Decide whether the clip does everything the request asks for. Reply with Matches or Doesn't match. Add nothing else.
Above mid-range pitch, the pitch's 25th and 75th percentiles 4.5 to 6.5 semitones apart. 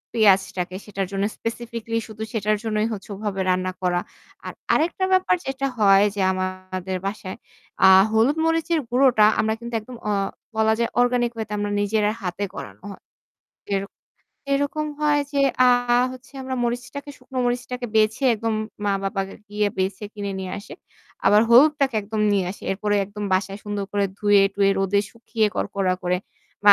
Doesn't match